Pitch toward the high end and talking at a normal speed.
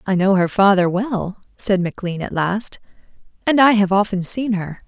Yes: high, 200 Hz; average, 185 wpm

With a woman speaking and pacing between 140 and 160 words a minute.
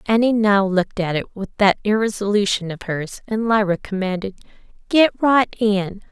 Yes: female; average, 155 wpm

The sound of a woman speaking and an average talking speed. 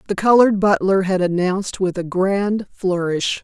Yes: female; average, 155 wpm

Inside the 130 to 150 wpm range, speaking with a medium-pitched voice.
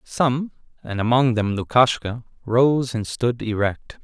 No: slow, 135 wpm; low, 120 Hz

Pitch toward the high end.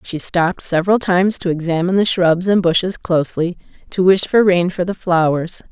No: medium, 180 Hz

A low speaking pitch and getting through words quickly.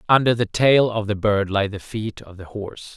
Yes: low, 105 Hz; fast, 245 wpm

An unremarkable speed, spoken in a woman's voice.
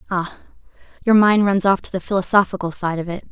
Yes: average, 180 wpm; female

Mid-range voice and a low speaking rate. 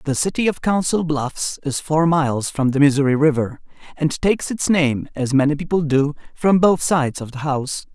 No: medium, 150 Hz; average, 195 wpm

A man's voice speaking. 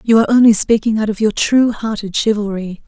No: female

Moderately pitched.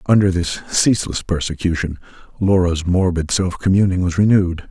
No: very low, 90 Hz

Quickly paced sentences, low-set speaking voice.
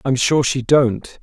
No: average, 195 wpm; low, 130 Hz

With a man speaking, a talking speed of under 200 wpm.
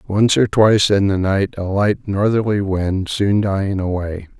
Yes: male; average, 180 wpm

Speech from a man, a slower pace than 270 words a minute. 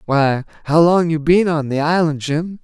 Yes: male; fast, 205 wpm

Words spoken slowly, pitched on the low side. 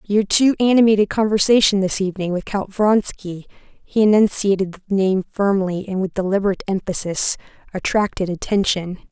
No: slow, 130 wpm; high, 195 Hz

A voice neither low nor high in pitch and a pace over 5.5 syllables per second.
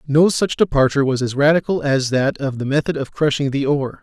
Yes: medium, 145 Hz; 5.9 syllables/s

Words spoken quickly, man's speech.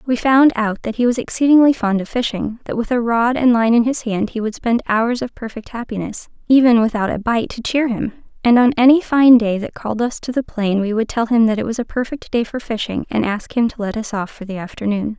No: fast, 255 wpm; female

